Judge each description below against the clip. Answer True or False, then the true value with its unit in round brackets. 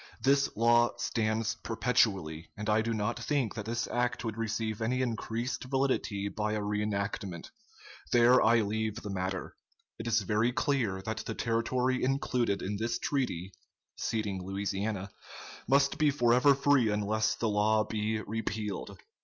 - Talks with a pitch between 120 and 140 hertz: False (110 Hz)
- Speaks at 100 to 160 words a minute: True (145 wpm)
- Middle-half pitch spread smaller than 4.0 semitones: True (2.7 semitones)